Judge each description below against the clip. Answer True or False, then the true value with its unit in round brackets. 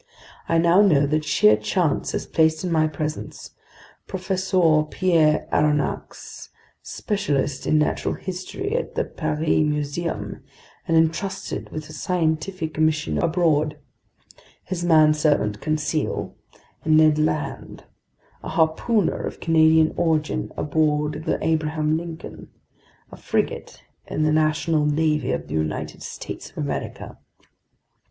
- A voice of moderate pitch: True (155 Hz)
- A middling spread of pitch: False (1.7 semitones)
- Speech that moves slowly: True (120 wpm)